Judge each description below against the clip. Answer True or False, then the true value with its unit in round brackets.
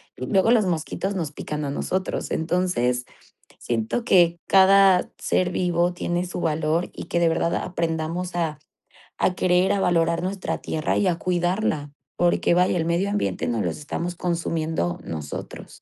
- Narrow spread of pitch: True (2.2 semitones)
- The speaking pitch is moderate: True (175 Hz)